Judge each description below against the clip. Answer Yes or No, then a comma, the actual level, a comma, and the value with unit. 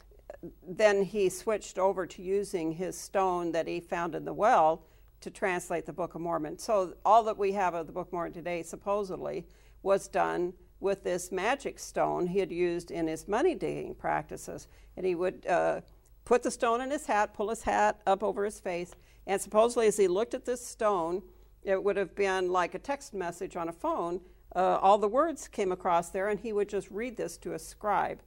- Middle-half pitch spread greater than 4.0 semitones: No, average, 2.9 semitones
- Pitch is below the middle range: No, high, 195 Hz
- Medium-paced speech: No, fast, 210 wpm